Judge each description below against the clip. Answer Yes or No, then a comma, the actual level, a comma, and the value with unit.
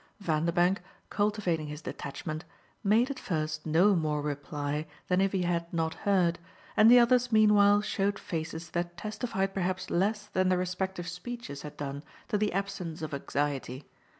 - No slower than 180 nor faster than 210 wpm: No, average, 155 wpm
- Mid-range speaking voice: Yes, medium, 180 Hz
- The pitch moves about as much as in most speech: Yes, average, 4.5 semitones